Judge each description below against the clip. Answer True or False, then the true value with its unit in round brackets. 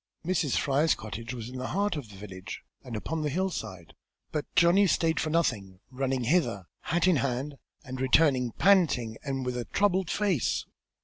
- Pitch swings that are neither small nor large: False (5.9 semitones)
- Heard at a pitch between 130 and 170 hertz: True (135 Hz)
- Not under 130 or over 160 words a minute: False (175 wpm)